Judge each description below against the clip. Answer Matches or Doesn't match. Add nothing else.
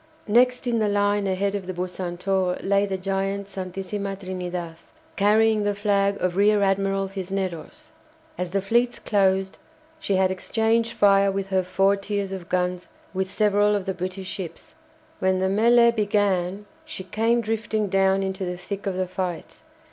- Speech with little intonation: Matches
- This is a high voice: Matches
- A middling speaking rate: Matches